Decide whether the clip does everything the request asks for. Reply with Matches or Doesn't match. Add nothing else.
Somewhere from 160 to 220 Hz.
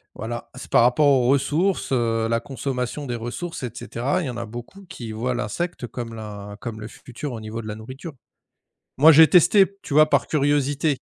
Doesn't match